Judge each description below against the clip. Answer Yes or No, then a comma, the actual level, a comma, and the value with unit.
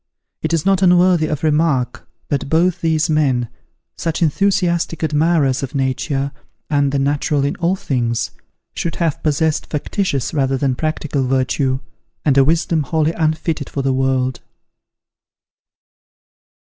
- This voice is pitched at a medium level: Yes, medium, 150 Hz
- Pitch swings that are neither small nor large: Yes, average, 3.3 semitones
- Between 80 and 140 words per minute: Yes, slow, 135 wpm